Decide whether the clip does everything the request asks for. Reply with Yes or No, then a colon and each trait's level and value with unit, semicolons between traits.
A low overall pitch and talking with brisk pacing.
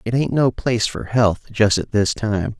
Yes: low, 110 Hz; fast, 230 wpm